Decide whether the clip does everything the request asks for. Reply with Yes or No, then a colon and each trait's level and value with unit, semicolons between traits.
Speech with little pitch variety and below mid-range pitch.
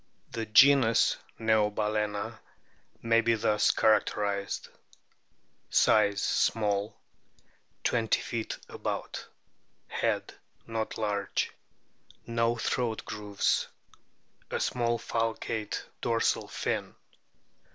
Yes: narrow, 1.6 semitones; low, 110 Hz